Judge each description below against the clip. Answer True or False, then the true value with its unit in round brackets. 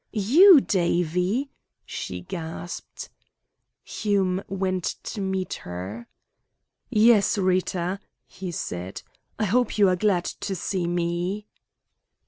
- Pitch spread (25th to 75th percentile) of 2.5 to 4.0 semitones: True (2.9 semitones)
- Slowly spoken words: True (105 wpm)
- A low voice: False (185 Hz)